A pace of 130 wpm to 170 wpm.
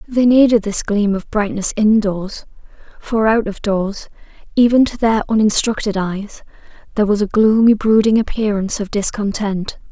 Yes: average, 150 wpm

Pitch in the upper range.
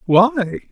Yes: high, 215 Hz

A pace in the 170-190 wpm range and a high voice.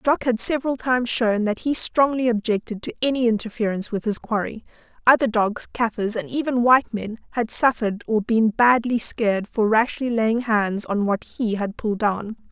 Yes: average, 180 wpm; high, 225 Hz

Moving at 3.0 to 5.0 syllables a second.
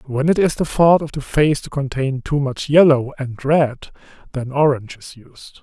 Yes: 4.6 syllables/s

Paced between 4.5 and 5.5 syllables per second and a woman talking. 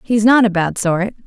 Yes: 4.7 syllables/s; female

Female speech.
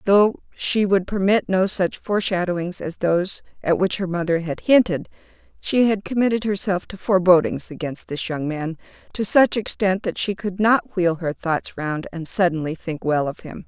Yes: female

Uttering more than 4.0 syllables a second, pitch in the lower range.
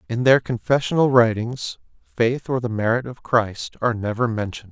Yes: 5.2 syllables/s; low, 120 Hz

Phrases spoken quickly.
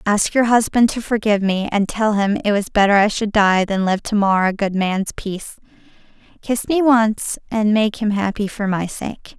Yes: fast, 210 wpm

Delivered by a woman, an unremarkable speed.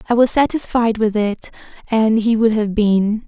Yes: female; average, 185 wpm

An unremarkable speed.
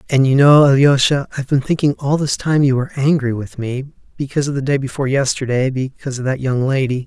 No: fast, 220 wpm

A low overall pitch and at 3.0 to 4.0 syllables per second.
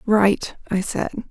No: high, 205 Hz; 3.4 syllables/s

